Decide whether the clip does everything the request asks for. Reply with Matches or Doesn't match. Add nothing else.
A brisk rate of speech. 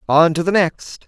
Matches